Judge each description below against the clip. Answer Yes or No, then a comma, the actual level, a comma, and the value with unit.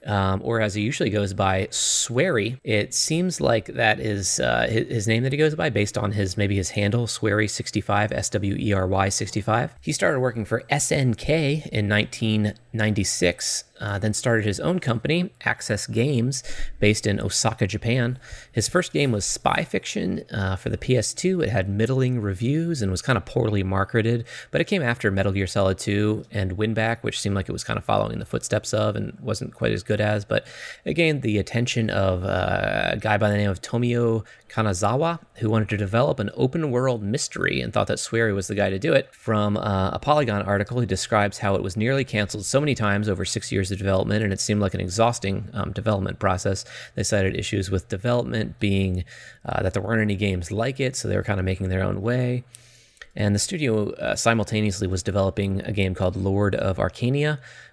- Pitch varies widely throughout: No, average, 3.1 semitones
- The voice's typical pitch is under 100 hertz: No, low, 105 Hz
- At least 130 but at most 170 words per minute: No, average, 200 wpm